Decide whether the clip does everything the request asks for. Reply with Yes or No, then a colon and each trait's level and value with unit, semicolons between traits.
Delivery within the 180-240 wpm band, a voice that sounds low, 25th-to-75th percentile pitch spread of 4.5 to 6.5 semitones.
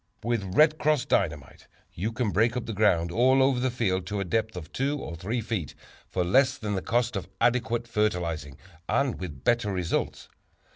Yes: average, 190 wpm; low, 110 Hz; average, 5.1 semitones